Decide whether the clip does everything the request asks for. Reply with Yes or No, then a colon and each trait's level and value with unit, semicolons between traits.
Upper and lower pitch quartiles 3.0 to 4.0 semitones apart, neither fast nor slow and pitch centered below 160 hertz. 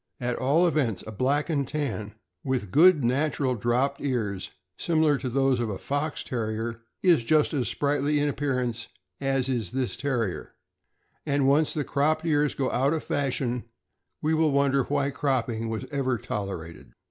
Yes: average, 3.6 semitones; average, 160 wpm; low, 135 Hz